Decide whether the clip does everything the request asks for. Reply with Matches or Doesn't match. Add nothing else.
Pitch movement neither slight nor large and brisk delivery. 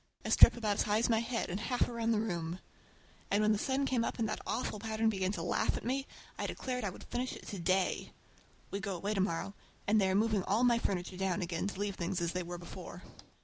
Matches